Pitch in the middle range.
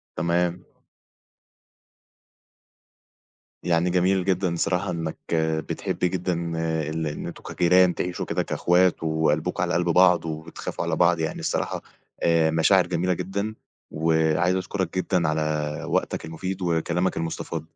No: very low, 85 Hz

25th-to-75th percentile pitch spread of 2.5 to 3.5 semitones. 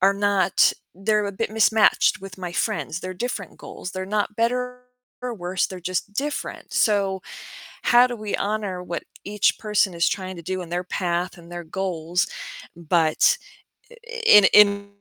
Yes: average, 2.8 semitones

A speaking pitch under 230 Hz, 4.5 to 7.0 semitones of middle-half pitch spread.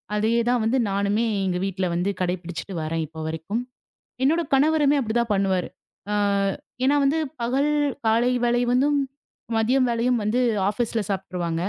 Yes: high, 220 Hz; average, 5.1 semitones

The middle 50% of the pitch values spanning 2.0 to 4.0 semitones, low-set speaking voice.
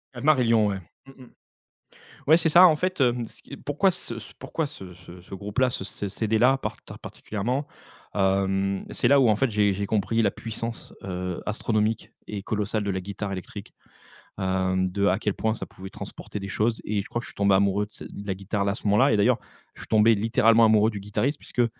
Yes: average, 3.3 semitones; low, 105 Hz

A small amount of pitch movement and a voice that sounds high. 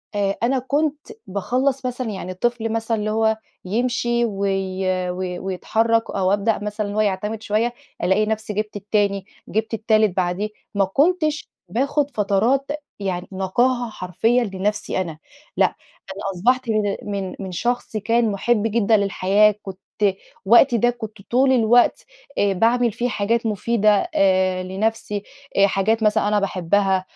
No: average, 3.2 semitones; high, 215 Hz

